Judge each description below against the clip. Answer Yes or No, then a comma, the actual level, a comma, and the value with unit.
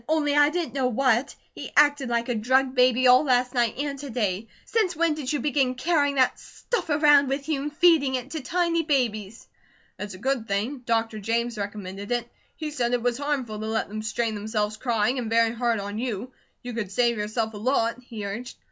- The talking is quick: Yes, fast, 210 wpm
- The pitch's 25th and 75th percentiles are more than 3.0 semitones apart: Yes, average, 4.1 semitones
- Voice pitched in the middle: No, high, 245 Hz